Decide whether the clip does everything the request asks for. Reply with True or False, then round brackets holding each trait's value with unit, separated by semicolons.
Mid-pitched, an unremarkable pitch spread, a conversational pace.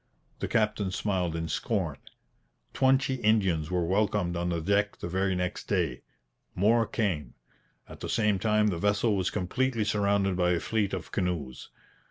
False (95 Hz; 3.2 semitones; 160 wpm)